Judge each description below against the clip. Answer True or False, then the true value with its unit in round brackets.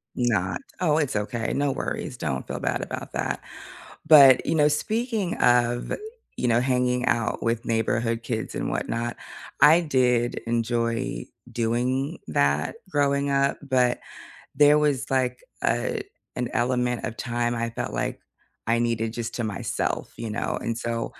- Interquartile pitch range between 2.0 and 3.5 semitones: True (2.9 semitones)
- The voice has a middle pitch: False (120 Hz)